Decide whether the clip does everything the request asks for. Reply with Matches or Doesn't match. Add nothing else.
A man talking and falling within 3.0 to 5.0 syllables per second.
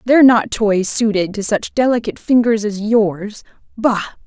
Doesn't match